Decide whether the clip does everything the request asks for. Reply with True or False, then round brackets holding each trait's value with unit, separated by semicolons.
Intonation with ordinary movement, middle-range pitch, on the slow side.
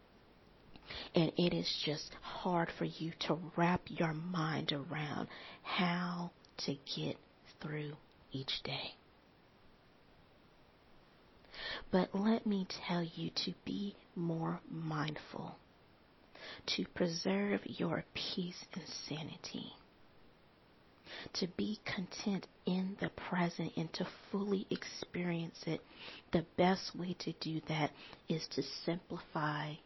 True (3.0 semitones; 170 Hz; 105 wpm)